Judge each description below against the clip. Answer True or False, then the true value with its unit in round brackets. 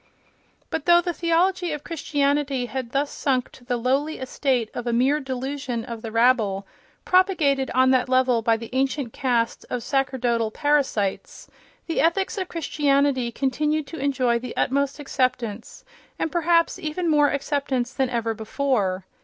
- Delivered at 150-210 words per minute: True (155 wpm)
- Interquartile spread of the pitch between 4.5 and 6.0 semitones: False (3.5 semitones)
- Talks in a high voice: True (265 Hz)